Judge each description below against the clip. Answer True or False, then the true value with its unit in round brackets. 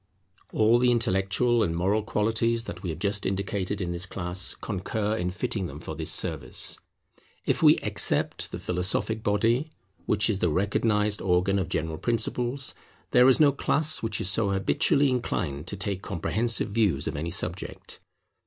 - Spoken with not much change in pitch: False (3.9 semitones)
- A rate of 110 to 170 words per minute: True (165 wpm)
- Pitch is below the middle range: True (105 Hz)